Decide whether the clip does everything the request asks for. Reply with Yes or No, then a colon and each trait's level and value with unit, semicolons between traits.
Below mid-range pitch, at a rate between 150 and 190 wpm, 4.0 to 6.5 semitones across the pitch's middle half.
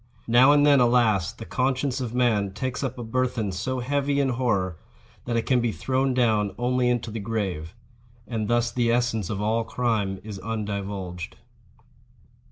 No: low, 115 Hz; average, 170 wpm; average, 3.4 semitones